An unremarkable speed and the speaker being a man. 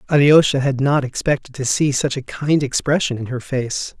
Yes: average, 195 wpm; male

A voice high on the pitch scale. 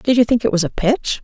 Yes: high, 225 Hz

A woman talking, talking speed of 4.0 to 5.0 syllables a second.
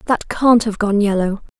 Yes: female; 4.7 syllables/s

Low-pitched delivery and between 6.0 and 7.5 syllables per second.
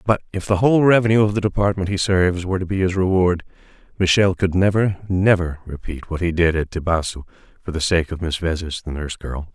Yes: very low, 90 Hz; 6.2 syllables/s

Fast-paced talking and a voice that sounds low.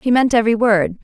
No: fast, 230 wpm; high, 225 Hz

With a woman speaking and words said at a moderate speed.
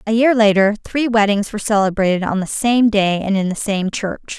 No: female; fast, 220 wpm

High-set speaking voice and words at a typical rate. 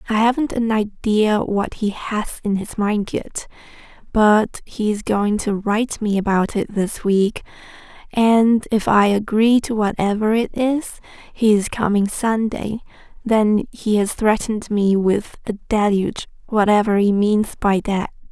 Yes: high, 215 Hz; average, 150 wpm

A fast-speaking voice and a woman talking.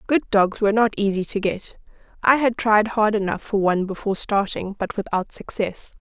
No: average, 190 wpm; female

